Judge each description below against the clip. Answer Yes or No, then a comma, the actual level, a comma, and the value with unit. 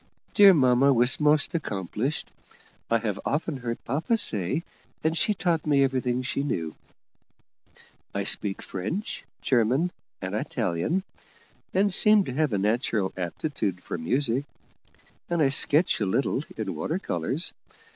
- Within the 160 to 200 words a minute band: No, slow, 135 wpm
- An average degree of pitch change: No, wide, 6.6 semitones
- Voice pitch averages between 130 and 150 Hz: Yes, low, 135 Hz